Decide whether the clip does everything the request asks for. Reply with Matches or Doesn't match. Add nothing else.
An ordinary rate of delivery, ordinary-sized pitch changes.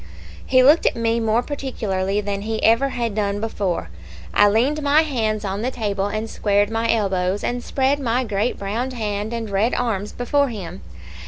Matches